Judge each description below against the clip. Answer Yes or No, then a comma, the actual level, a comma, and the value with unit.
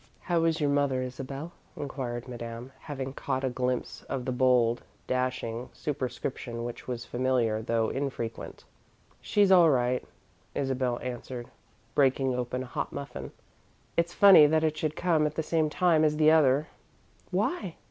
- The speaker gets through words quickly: No, average, 150 wpm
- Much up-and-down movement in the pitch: No, average, 3.8 semitones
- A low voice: Yes, low, 130 Hz